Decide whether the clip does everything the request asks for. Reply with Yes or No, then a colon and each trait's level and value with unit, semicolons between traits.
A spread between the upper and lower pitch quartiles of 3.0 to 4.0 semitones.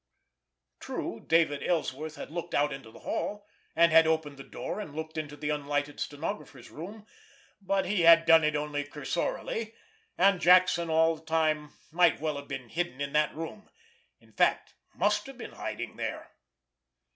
Yes: average, 3.3 semitones